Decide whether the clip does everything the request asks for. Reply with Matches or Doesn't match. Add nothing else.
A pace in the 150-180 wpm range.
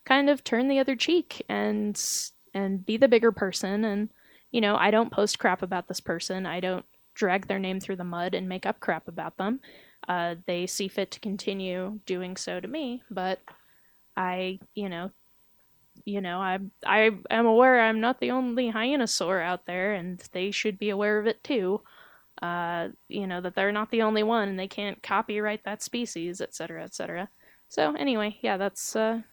Doesn't match